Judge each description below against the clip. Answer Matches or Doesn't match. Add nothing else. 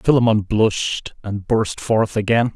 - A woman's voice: Doesn't match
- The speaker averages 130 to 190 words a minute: Matches